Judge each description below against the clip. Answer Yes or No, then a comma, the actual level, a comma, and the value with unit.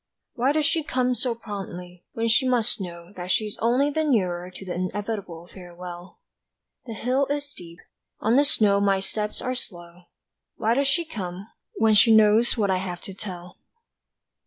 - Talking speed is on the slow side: No, average, 175 wpm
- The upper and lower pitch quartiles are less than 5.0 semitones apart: No, wide, 5.5 semitones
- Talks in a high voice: Yes, high, 210 Hz